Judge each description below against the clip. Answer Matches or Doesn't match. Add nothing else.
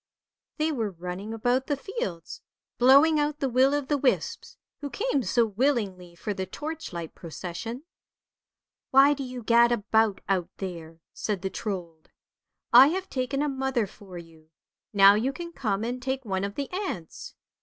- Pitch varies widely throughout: Matches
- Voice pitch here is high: Matches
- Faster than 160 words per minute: Matches